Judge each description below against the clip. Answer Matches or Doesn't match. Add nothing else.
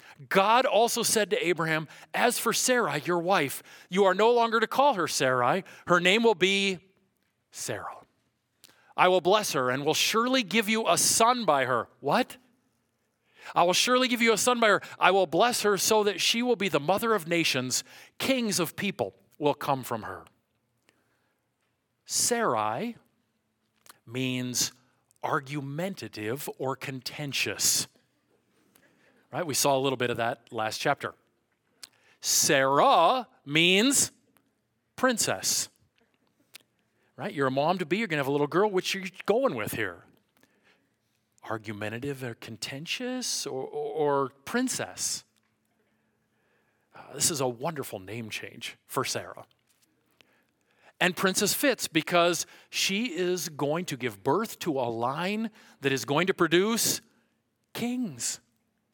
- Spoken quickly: Doesn't match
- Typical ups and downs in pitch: Doesn't match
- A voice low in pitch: Doesn't match